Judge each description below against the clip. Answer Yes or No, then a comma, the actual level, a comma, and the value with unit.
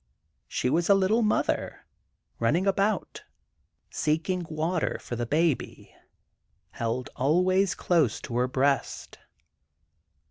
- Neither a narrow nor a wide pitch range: No, wide, 6.3 semitones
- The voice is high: No, medium, 160 Hz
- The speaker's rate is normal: No, slow, 105 wpm